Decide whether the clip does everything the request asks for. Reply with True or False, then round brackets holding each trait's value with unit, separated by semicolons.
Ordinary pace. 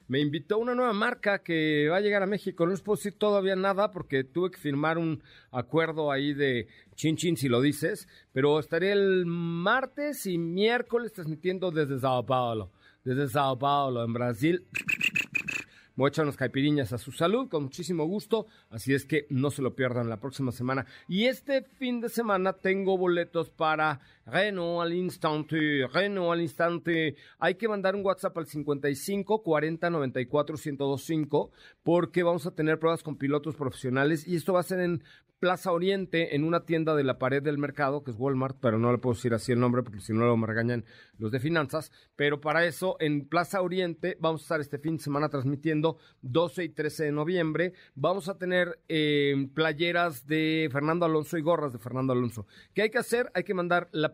False (195 wpm)